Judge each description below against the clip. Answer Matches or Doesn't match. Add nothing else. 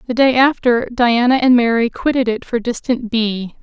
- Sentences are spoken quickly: Doesn't match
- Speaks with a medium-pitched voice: Doesn't match